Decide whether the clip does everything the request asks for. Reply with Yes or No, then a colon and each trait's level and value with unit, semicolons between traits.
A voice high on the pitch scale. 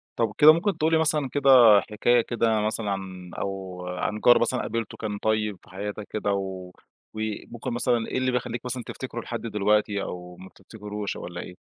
No: low, 110 Hz